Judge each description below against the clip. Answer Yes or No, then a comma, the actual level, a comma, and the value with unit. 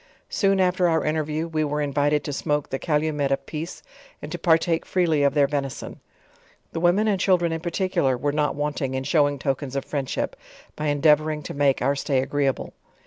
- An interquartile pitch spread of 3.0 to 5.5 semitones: No, narrow, 2.5 semitones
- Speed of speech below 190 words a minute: No, average, 195 wpm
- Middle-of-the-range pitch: Yes, medium, 150 Hz